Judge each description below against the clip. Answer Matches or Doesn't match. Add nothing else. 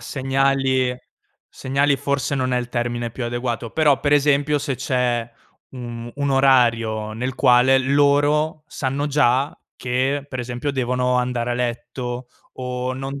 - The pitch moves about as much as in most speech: Doesn't match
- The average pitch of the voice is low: Matches